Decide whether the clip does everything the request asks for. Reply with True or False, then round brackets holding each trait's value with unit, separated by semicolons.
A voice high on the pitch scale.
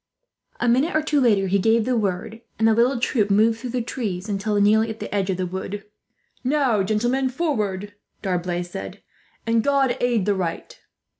True (220 Hz)